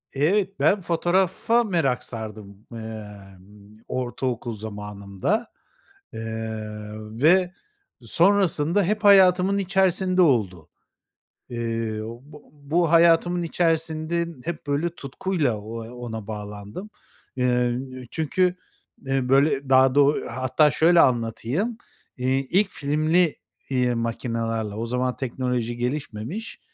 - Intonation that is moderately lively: No, wide, 7.3 semitones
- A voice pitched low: Yes, low, 130 Hz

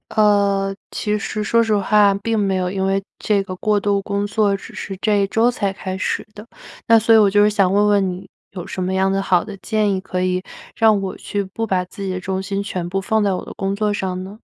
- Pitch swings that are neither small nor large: No, narrow, 1.6 semitones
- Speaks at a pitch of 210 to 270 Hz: No, high, 200 Hz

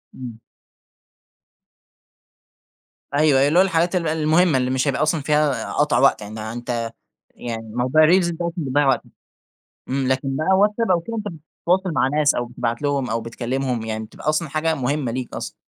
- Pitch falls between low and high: Yes, medium, 145 Hz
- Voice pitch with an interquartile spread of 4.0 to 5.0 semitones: Yes, average, 4.5 semitones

